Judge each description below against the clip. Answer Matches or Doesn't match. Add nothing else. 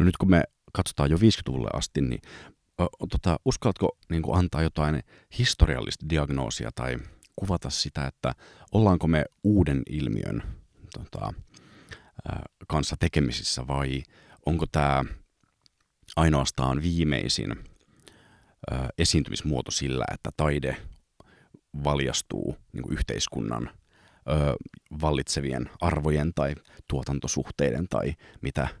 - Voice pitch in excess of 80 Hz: Doesn't match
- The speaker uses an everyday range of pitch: Matches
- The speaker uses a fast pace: Doesn't match